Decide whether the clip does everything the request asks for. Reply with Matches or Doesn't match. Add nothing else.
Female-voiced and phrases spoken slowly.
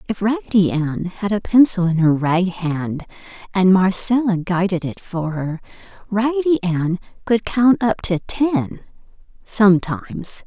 Matches